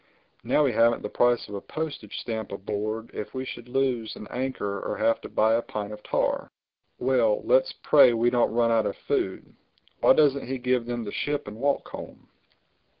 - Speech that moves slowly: No, average, 190 wpm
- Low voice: Yes, low, 120 Hz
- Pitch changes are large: No, average, 3.5 semitones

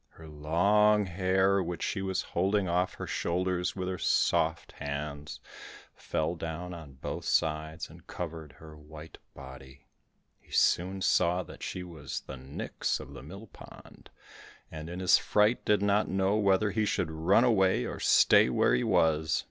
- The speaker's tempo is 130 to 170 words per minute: Yes, average, 165 wpm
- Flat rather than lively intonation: No, average, 3.7 semitones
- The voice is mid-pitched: No, very low, 85 Hz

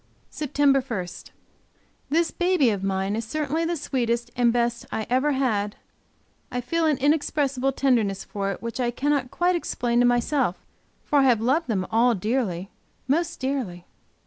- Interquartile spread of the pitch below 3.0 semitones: No, average, 4.3 semitones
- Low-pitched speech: No, very high, 250 Hz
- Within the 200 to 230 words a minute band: No, average, 160 wpm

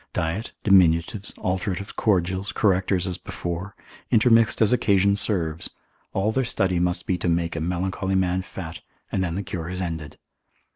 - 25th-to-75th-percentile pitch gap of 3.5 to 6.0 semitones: No, narrow, 2.4 semitones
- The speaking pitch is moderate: No, very low, 95 Hz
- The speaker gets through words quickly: No, average, 155 wpm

